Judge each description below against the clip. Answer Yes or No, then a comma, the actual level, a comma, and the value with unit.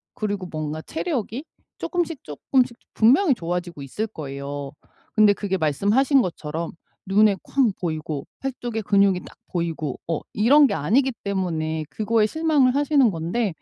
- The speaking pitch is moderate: No, high, 200 Hz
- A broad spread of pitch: Yes, wide, 7.8 semitones